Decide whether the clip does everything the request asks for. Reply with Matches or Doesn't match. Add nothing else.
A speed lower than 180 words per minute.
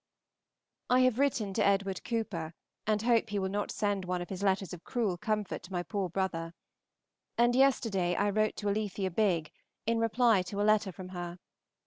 Doesn't match